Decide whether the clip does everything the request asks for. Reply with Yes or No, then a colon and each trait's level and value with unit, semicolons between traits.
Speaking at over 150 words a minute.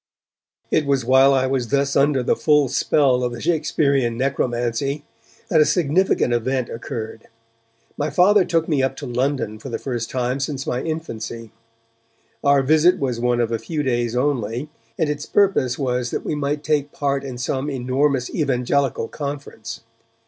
Yes: average, 165 wpm